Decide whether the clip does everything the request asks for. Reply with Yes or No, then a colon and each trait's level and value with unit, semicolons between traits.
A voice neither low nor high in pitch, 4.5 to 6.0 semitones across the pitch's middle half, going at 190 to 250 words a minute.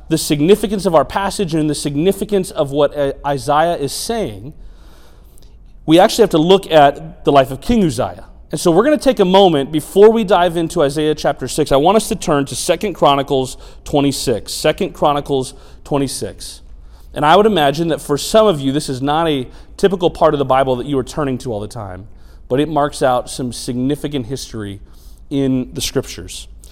Yes: medium, 145 Hz; average, 4.9 semitones; average, 195 wpm